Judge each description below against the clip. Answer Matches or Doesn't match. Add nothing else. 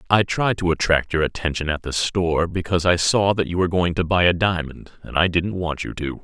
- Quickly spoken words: Matches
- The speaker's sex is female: Doesn't match